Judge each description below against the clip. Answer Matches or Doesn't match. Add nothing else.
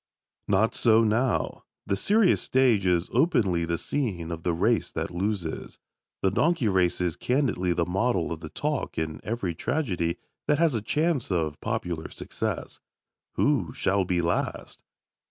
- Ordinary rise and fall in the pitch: Doesn't match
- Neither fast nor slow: Matches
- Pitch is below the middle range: Matches